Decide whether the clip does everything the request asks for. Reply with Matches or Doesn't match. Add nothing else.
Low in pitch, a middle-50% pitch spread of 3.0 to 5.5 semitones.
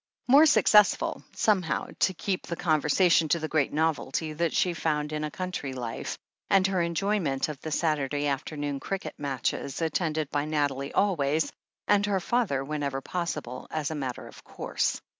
Doesn't match